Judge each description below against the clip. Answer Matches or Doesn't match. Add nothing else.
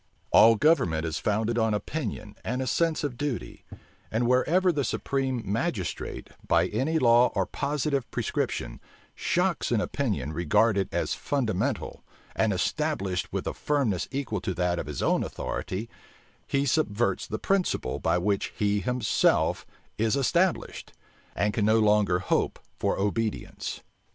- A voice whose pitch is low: Matches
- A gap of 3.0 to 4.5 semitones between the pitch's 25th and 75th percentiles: Doesn't match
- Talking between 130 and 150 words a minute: Matches